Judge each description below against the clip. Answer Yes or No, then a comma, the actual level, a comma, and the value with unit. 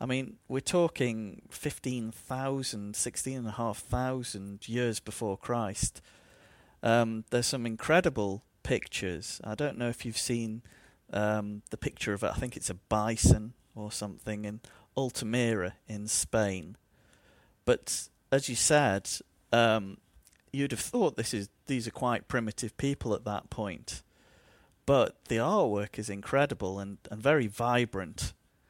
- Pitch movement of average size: Yes, average, 3.5 semitones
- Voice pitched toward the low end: Yes, low, 115 Hz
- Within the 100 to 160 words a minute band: Yes, average, 140 wpm